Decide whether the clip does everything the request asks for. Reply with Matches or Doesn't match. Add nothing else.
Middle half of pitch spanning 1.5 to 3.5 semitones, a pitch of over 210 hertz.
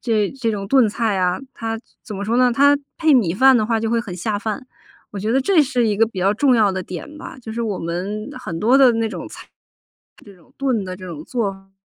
Doesn't match